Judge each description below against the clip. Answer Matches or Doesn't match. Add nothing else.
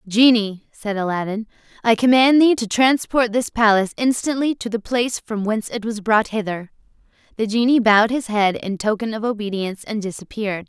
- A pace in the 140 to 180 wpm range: Matches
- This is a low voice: Doesn't match